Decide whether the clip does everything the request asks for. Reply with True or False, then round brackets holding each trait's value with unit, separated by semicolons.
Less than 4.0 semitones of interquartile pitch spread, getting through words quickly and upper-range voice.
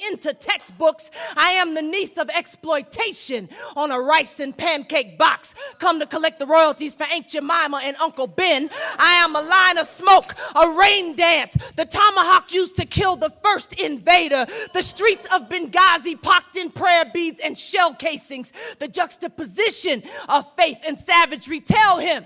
False (3.2 semitones; 165 wpm; 330 Hz)